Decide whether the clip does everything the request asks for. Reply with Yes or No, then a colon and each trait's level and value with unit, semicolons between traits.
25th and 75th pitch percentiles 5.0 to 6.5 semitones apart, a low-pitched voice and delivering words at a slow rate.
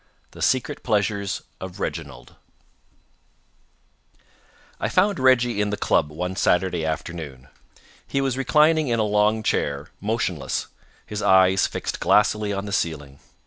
Yes: average, 5.3 semitones; low, 100 Hz; slow, 130 wpm